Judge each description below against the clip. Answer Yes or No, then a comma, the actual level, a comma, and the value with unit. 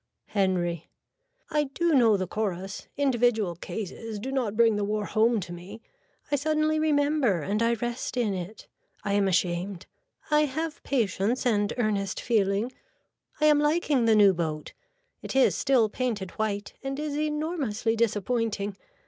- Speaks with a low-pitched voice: No, high, 225 Hz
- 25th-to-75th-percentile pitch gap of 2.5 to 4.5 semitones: No, average, 5.3 semitones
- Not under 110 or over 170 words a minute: Yes, average, 150 wpm